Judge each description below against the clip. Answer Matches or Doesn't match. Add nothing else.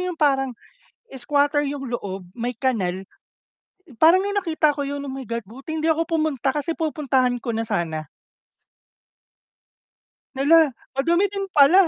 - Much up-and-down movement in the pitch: Doesn't match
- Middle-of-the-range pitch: Doesn't match